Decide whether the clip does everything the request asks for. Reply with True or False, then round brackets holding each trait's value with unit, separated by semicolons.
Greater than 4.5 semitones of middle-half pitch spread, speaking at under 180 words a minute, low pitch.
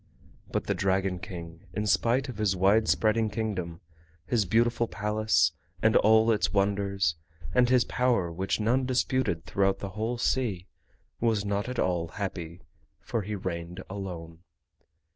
False (3.7 semitones; 145 wpm; 100 Hz)